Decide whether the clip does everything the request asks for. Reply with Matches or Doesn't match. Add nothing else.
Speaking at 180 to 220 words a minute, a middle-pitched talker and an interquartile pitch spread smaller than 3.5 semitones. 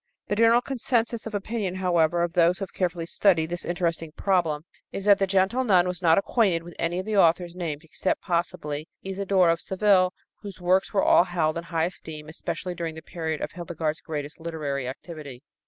Matches